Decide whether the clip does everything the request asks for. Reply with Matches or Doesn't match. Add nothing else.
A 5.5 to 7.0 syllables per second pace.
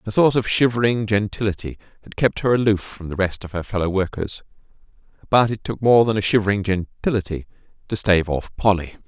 Matches